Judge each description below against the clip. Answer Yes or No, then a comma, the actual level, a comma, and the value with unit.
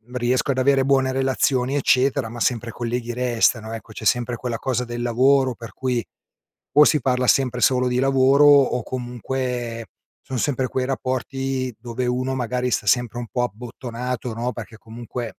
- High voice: No, low, 125 Hz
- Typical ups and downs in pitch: No, narrow, 1.7 semitones